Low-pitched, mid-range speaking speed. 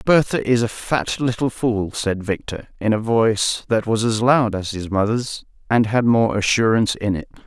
Yes: low, 110 Hz; average, 195 wpm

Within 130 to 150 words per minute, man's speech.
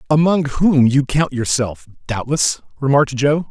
Yes: slow, 135 wpm; male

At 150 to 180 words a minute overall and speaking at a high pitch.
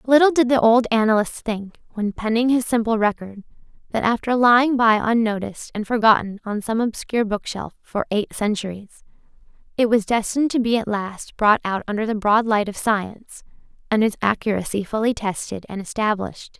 Yes: average, 170 wpm; high, 220 Hz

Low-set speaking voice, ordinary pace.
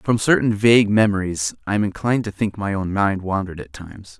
No: low, 100 Hz; fast, 215 wpm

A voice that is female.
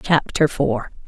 Yes: female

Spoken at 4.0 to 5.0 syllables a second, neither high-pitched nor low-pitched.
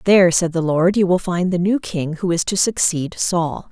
Yes: 4.8 syllables/s; medium, 175 Hz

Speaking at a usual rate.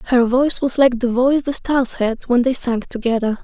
No: fast, 225 wpm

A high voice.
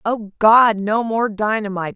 Yes: high, 215 Hz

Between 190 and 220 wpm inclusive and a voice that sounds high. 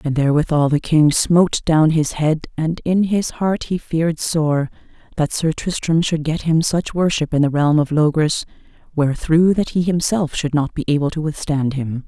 No: average, 195 wpm; medium, 155 Hz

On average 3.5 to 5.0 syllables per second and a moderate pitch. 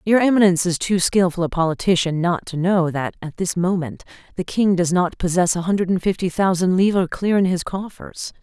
No: 5.5 syllables/s; medium, 180 Hz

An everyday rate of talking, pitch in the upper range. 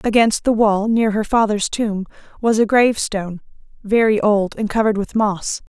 Yes: average, 165 wpm; high, 215 Hz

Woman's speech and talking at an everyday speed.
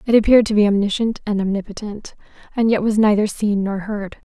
Yes: female; average, 195 wpm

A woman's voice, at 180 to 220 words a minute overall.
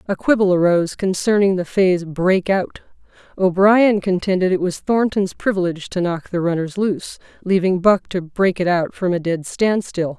No: female; average, 170 wpm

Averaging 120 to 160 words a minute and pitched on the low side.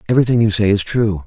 No: fast, 240 wpm; low, 110 Hz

